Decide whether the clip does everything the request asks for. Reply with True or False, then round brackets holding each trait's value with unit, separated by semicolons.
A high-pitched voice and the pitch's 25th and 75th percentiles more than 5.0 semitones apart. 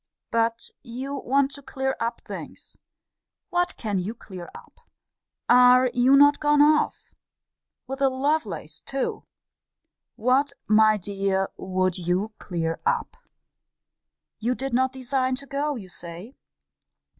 True (250 Hz; 5.5 semitones)